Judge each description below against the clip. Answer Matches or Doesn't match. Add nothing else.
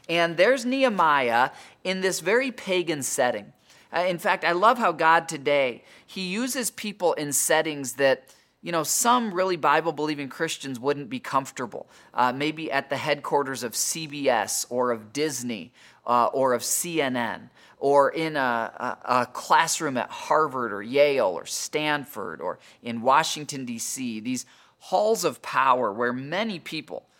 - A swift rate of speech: Doesn't match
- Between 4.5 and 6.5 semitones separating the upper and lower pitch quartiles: Matches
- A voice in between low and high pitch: Matches